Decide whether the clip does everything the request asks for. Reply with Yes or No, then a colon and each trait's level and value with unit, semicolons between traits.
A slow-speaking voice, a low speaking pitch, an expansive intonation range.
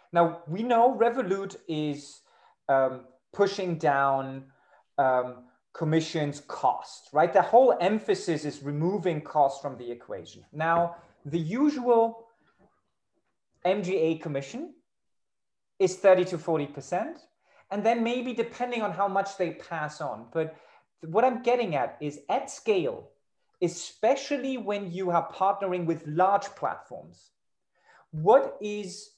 No: slow, 120 wpm; medium, 175 Hz; wide, 5.7 semitones